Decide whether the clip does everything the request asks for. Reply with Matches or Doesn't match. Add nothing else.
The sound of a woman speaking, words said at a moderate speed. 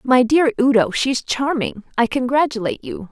Matches